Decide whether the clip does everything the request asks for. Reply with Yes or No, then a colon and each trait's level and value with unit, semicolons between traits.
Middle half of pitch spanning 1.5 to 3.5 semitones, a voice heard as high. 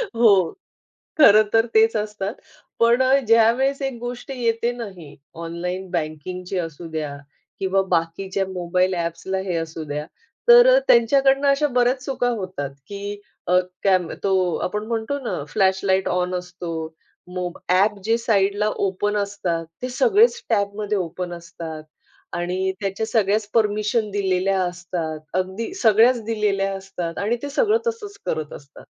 No: average, 4.2 semitones; high, 195 Hz